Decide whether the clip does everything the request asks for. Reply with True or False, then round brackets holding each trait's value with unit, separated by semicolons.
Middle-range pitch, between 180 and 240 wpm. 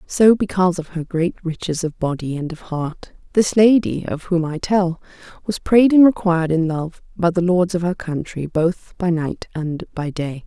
True (175 Hz; 200 wpm)